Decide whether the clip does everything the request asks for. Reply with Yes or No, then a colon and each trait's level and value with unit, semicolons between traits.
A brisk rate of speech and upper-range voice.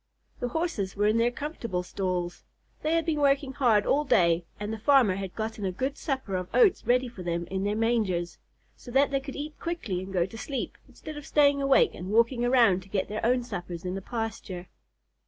Yes: fast, 215 wpm; high, 225 Hz